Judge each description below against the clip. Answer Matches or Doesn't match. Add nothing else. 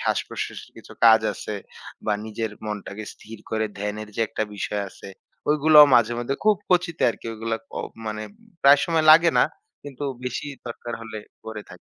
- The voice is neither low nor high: Doesn't match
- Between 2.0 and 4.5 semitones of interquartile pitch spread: Doesn't match